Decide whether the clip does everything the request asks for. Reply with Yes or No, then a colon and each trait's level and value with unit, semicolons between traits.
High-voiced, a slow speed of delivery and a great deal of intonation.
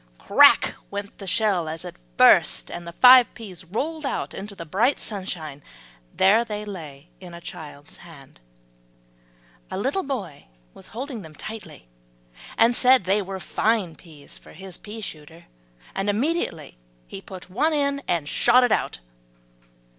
No: high, 195 Hz; average, 155 wpm; wide, 5.7 semitones